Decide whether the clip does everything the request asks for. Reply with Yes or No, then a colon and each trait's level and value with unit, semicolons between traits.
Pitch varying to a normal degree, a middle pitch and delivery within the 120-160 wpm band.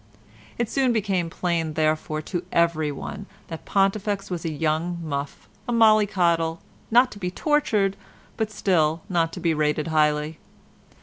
Yes: average, 4.3 semitones; medium, 170 Hz; average, 140 wpm